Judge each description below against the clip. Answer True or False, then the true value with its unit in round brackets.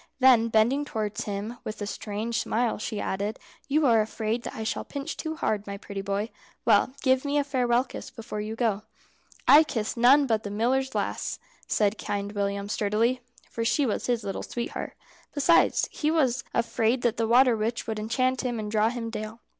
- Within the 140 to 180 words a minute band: False (195 wpm)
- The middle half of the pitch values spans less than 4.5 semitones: True (3.1 semitones)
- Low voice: False (230 Hz)